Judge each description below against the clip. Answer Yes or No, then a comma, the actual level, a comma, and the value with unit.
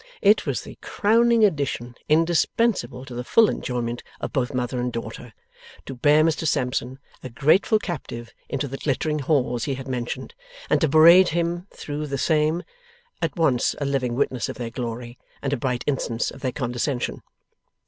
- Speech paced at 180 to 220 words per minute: No, average, 170 wpm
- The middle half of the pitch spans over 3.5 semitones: Yes, average, 4.5 semitones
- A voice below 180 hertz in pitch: Yes, low, 135 Hz